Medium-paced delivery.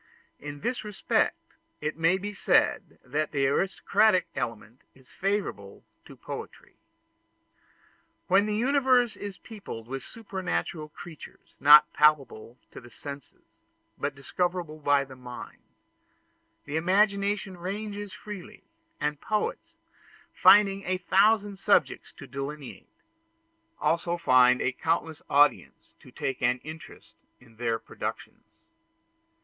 No: slow, 115 wpm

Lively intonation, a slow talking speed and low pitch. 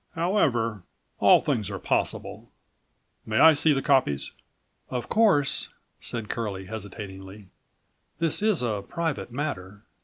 Yes: wide, 7.2 semitones; slow, 120 wpm; low, 115 Hz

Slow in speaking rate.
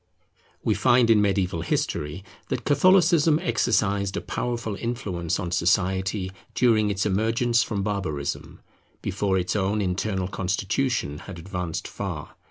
Yes: slow, 125 wpm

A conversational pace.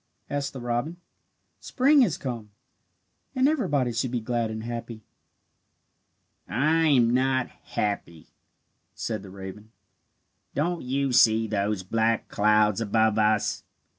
No: slow, 120 wpm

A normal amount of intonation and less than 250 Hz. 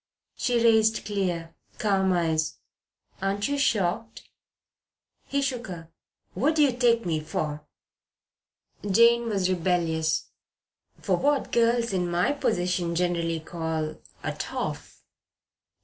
No: wide, 5.7 semitones; high, 190 Hz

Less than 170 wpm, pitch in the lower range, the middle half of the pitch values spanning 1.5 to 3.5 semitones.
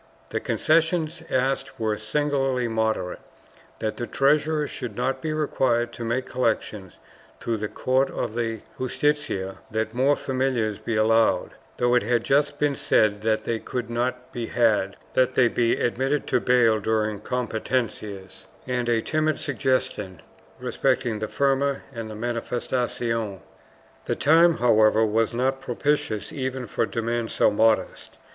Yes: average, 150 wpm; low, 120 Hz; average, 3.2 semitones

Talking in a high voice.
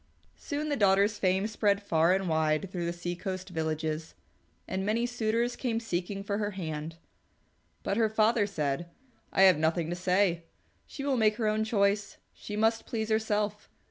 Yes: high, 200 Hz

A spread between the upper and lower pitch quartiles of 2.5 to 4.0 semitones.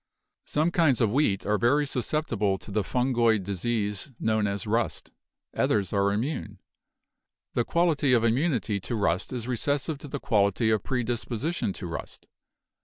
No: average, 4.8 semitones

